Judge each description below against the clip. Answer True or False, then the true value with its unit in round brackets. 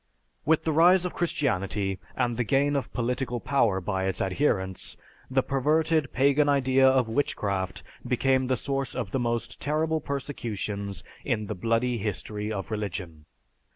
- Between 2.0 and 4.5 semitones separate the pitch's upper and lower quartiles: False (5.5 semitones)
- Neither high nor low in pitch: False (125 Hz)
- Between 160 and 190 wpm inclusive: False (150 wpm)